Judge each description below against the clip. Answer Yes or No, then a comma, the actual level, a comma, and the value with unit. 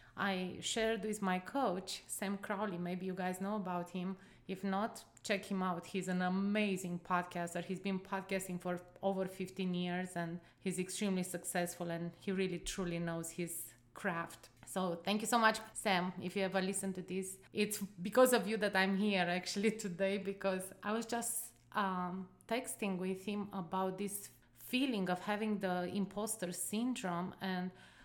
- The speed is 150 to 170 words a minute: Yes, average, 165 wpm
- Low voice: No, high, 190 Hz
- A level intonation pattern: Yes, narrow, 2.1 semitones